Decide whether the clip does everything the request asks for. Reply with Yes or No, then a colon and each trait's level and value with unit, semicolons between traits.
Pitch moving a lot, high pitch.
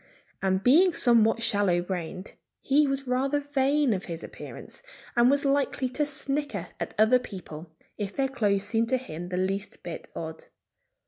Yes: wide, 6.0 semitones; high, 240 Hz